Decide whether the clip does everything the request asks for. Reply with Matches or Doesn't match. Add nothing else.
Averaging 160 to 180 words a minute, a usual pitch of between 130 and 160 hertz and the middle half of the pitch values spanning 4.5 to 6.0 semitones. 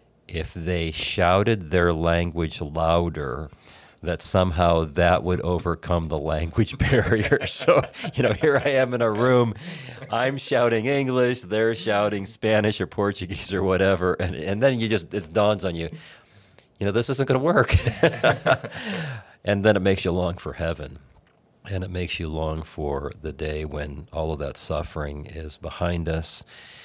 Doesn't match